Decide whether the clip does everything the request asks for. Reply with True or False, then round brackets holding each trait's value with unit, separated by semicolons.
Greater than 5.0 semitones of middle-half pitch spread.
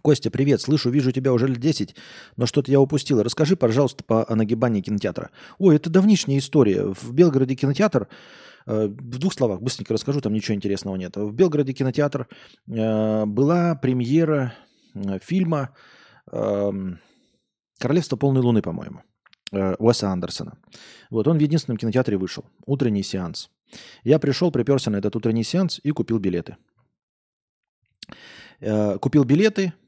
True (5.5 semitones)